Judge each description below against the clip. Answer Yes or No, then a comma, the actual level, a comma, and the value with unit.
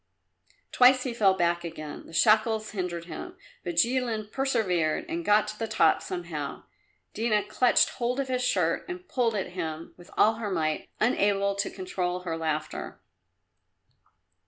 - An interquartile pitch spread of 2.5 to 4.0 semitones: No, average, 5.3 semitones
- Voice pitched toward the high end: Yes, high, 205 Hz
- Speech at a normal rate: Yes, average, 155 wpm